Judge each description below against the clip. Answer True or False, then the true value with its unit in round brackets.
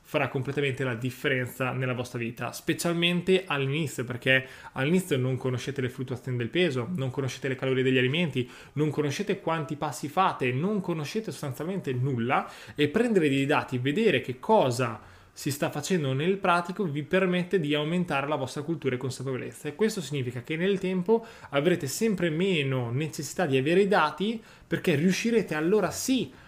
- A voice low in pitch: False (150 Hz)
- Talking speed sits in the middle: True (160 wpm)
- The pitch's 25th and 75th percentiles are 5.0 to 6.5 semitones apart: True (5.6 semitones)